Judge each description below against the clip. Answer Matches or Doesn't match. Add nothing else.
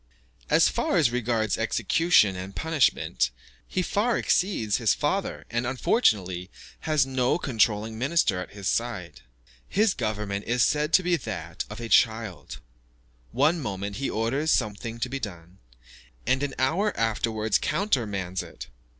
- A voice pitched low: Matches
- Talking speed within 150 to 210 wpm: Doesn't match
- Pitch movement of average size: Doesn't match